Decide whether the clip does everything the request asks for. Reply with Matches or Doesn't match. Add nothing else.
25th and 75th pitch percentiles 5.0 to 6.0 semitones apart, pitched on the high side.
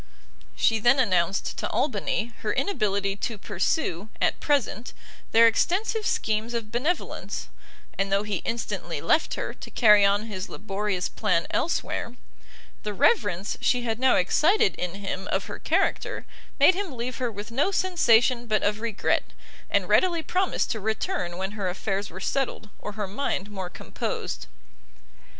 Doesn't match